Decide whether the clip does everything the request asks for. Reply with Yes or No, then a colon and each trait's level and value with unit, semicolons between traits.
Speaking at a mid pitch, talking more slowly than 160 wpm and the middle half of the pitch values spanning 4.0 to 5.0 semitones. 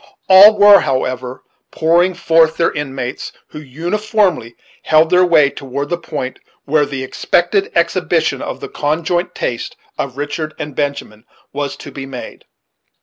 Yes: medium, 150 Hz; average, 145 wpm; average, 4.3 semitones